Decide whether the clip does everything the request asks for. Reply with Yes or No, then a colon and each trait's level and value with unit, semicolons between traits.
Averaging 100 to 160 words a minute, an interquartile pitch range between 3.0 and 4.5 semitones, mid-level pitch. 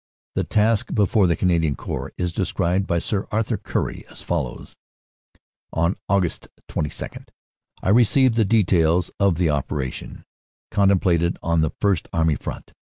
No: average, 140 wpm; average, 3.6 semitones; very low, 90 Hz